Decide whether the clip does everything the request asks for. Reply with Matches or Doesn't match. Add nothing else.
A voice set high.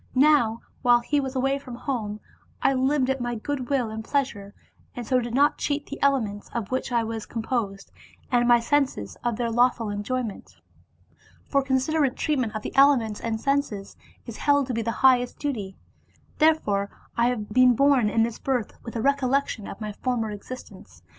Matches